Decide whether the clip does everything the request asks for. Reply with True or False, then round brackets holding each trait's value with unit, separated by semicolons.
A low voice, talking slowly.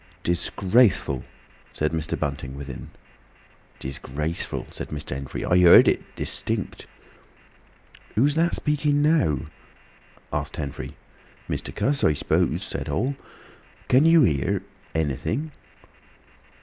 True (85 Hz; 95 wpm)